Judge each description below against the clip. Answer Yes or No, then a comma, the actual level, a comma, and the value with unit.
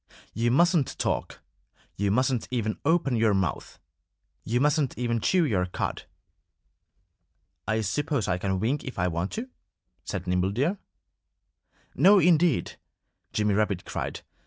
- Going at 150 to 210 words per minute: No, slow, 135 wpm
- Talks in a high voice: No, low, 115 Hz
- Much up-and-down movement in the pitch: Yes, wide, 7.0 semitones